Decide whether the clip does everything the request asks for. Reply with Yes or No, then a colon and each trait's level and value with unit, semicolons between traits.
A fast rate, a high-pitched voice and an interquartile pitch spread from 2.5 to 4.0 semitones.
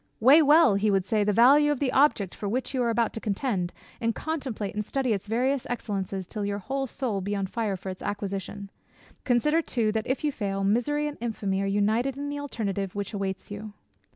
No: fast, 215 wpm; high, 220 Hz; average, 4.8 semitones